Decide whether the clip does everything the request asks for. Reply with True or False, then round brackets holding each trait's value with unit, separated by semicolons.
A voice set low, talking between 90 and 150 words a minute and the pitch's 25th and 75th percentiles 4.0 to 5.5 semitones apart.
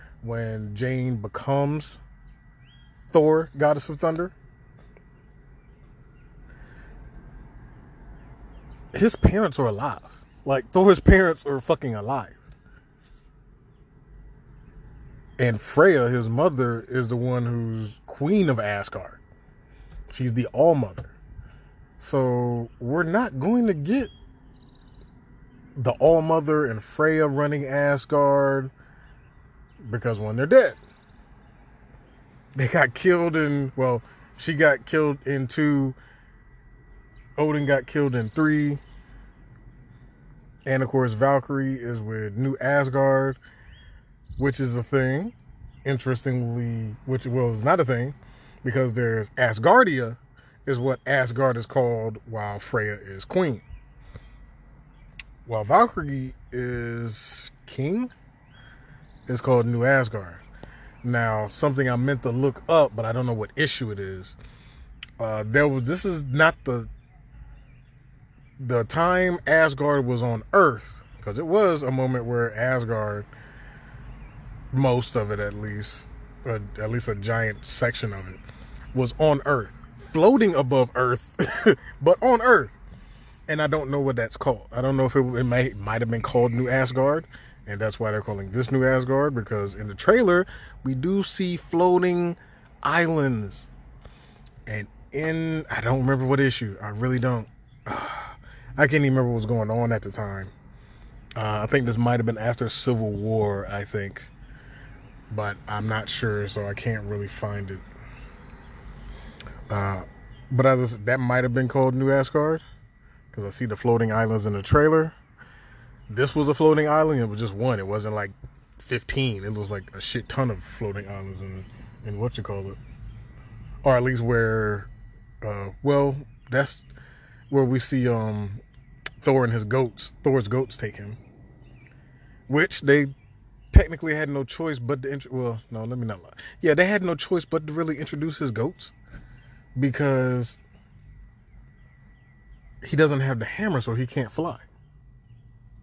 False (130 Hz; 140 wpm; 3.4 semitones)